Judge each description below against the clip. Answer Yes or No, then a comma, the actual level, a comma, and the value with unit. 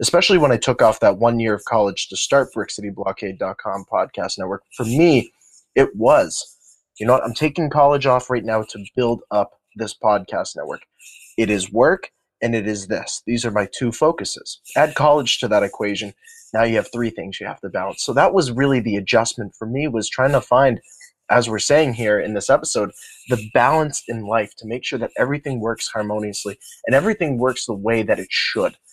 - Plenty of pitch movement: No, average, 4.6 semitones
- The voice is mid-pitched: No, low, 120 Hz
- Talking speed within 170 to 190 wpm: No, fast, 205 wpm